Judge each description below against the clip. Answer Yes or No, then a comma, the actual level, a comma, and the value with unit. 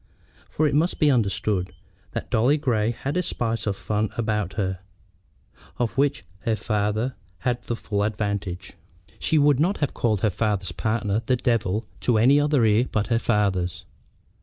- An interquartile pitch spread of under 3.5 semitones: No, average, 3.8 semitones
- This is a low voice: Yes, low, 110 Hz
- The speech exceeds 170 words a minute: No, average, 165 wpm